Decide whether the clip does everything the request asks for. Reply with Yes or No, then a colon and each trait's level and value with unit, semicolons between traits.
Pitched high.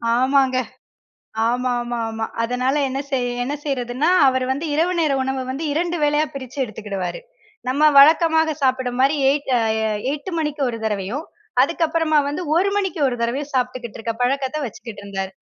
Yes: very high, 265 Hz